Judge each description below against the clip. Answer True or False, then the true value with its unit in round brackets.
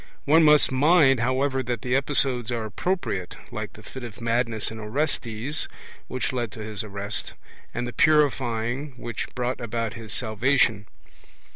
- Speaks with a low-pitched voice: True (120 Hz)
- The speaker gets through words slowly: False (150 wpm)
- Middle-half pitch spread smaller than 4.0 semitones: True (3.2 semitones)